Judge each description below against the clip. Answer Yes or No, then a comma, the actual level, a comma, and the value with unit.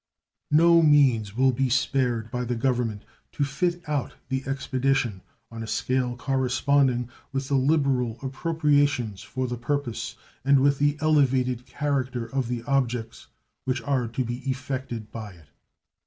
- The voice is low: Yes, low, 130 Hz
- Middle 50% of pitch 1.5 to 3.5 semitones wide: Yes, narrow, 2.6 semitones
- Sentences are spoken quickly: No, average, 145 wpm